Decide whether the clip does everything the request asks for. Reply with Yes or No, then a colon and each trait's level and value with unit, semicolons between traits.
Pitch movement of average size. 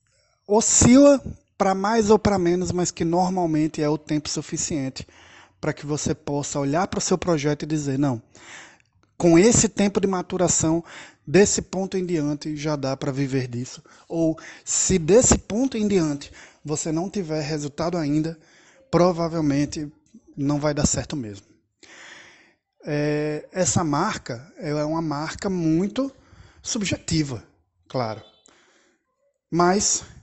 Yes: average, 4.0 semitones